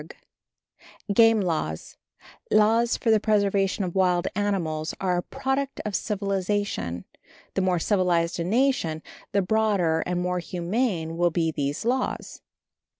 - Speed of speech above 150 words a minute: No, slow, 135 wpm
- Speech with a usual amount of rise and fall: Yes, average, 3.9 semitones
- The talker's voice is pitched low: No, high, 190 Hz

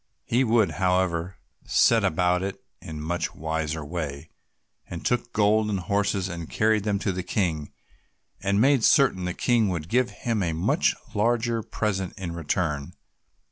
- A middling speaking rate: Yes, average, 160 wpm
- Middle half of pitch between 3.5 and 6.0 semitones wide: Yes, average, 4.6 semitones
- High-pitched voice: No, very low, 95 Hz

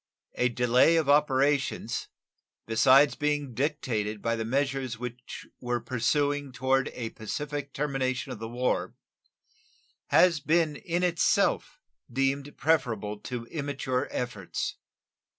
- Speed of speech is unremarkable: No, slow, 115 wpm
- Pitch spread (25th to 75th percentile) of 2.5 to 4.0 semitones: Yes, average, 3.1 semitones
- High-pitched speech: No, low, 135 Hz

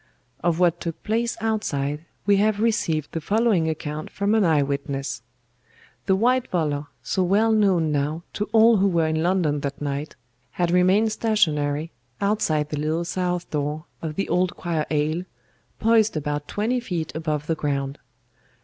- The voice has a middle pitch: Yes, medium, 170 Hz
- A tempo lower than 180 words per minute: Yes, average, 160 wpm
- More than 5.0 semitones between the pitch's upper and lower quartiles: Yes, wide, 5.5 semitones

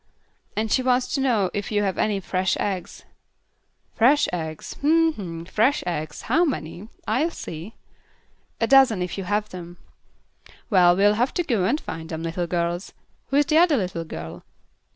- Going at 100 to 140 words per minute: No, average, 170 wpm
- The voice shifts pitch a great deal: Yes, wide, 6.8 semitones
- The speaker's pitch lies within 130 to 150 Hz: No, high, 200 Hz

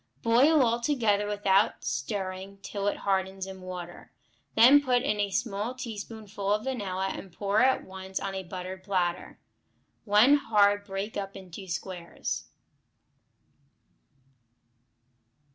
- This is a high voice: Yes, high, 200 Hz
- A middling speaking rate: No, slow, 125 wpm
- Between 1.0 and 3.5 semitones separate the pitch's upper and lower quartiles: Yes, average, 2.7 semitones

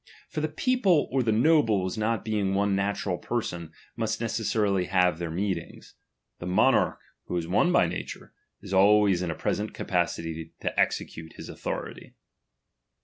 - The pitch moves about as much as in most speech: Yes, average, 3.9 semitones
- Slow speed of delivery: No, average, 155 wpm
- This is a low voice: Yes, low, 100 Hz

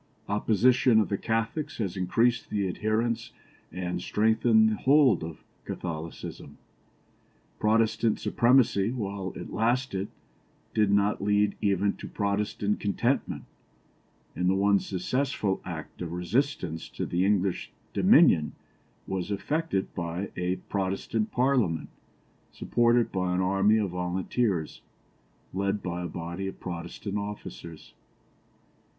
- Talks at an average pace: No, slow, 115 wpm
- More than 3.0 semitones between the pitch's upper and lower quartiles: Yes, average, 3.6 semitones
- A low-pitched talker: Yes, low, 100 Hz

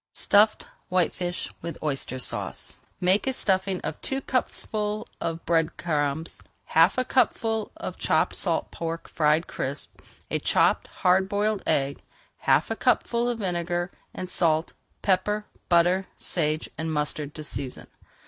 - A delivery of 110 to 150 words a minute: Yes, average, 140 wpm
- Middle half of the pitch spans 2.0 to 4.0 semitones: No, average, 4.5 semitones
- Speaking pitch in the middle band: Yes, medium, 175 Hz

